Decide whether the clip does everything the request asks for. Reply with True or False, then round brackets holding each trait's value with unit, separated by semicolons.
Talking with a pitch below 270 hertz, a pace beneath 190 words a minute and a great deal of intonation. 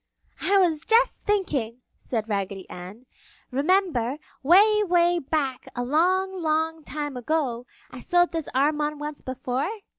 False (300 Hz; 140 wpm; 5.7 semitones)